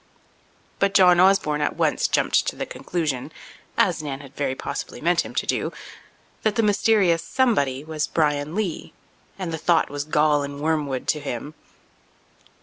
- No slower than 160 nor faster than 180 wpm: No, average, 150 wpm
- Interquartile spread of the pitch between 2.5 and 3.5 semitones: No, average, 3.9 semitones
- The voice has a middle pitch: Yes, medium, 155 Hz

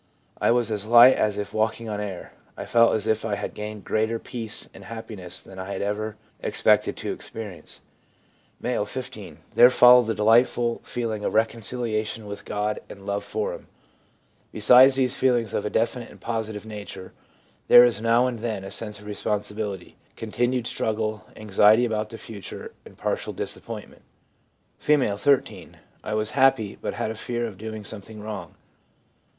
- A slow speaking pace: No, average, 170 wpm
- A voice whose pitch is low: Yes, low, 110 Hz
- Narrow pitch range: Yes, narrow, 2.1 semitones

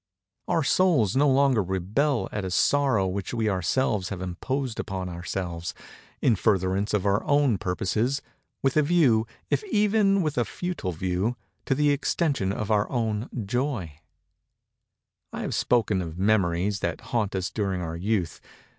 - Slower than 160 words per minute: Yes, average, 145 wpm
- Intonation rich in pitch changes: Yes, wide, 6.5 semitones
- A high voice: No, low, 105 Hz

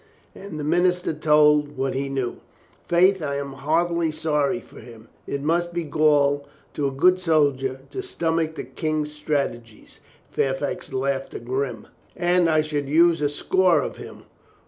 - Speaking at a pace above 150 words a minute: Yes, average, 160 wpm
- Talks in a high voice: No, medium, 150 Hz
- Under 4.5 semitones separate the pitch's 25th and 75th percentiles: Yes, average, 3.3 semitones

